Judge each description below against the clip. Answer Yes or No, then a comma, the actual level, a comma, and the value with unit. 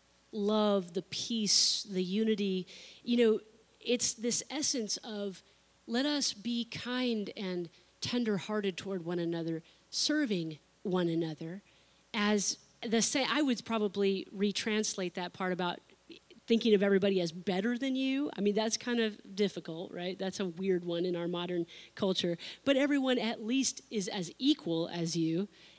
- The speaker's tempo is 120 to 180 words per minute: Yes, average, 150 wpm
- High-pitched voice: Yes, high, 205 Hz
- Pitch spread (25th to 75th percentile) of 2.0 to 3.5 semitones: No, average, 4.3 semitones